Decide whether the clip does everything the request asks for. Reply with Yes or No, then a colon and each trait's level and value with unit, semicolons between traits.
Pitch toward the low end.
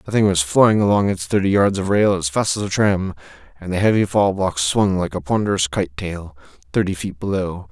Yes: very low, 95 Hz